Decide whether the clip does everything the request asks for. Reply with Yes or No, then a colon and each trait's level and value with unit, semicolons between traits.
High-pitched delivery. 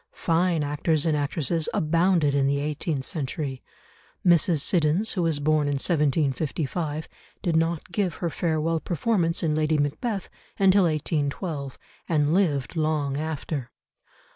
No: medium, 155 Hz